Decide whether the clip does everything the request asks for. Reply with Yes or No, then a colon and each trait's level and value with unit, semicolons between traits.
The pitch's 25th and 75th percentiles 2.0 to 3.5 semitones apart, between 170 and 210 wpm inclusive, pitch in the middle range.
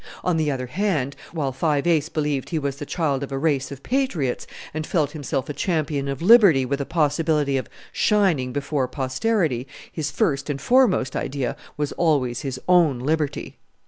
Yes: average, 3.2 semitones; average, 175 wpm; medium, 145 Hz